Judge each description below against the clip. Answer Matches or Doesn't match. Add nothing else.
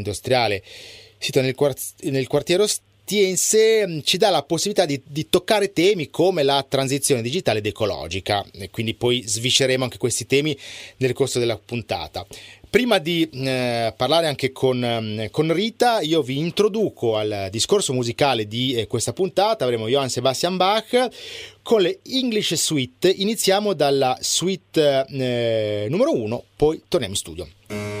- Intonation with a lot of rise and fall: Matches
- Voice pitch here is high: Doesn't match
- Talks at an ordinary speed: Matches